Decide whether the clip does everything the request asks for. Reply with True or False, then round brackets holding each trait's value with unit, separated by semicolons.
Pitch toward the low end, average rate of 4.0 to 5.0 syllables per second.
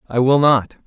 True (130 Hz; 4.9 syllables/s)